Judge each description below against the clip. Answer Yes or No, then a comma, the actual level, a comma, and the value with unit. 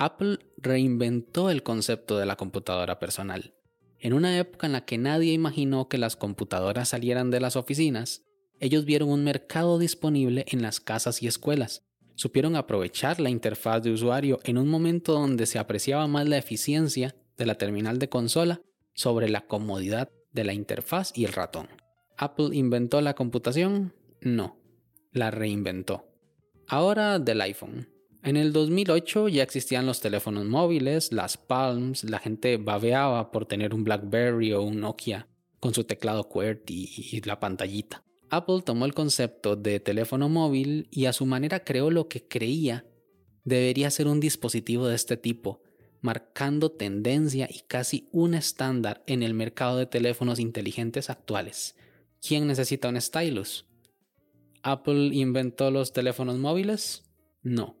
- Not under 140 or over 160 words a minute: Yes, average, 150 wpm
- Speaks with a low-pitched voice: Yes, low, 125 Hz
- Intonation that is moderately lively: Yes, average, 4.7 semitones